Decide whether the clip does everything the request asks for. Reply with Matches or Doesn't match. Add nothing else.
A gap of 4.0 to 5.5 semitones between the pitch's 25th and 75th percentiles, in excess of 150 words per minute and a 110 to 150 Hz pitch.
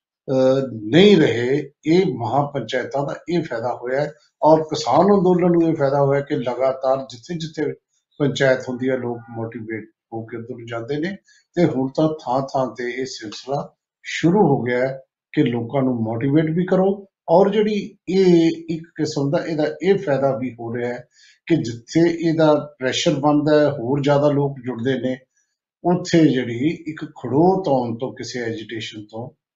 Matches